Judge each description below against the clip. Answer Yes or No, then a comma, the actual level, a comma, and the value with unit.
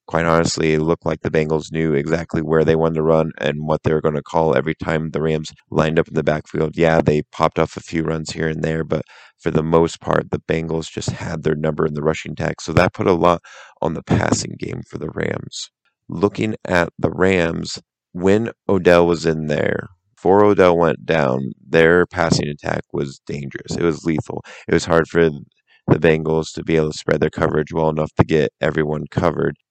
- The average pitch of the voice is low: Yes, very low, 80 Hz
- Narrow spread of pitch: Yes, narrow, 1.2 semitones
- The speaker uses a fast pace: Yes, fast, 215 wpm